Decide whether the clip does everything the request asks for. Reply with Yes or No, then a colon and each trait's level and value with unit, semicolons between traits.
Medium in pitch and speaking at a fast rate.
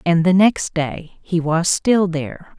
No: medium, 175 Hz; average, 185 wpm